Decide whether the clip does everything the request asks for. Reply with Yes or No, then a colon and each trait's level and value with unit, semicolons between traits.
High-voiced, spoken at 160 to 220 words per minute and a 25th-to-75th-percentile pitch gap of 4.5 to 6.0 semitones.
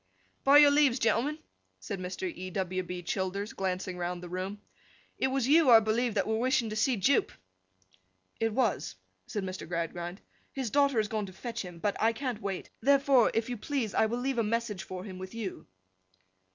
Yes: high, 220 Hz; average, 195 wpm; average, 5.1 semitones